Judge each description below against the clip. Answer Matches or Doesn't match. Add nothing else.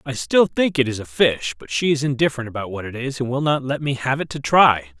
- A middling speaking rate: Doesn't match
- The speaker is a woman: Doesn't match